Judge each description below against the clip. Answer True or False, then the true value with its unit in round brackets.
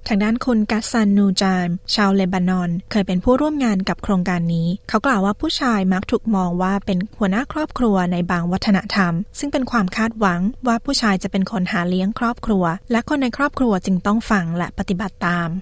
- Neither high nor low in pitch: False (200 Hz)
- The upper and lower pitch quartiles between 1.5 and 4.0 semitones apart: True (3.6 semitones)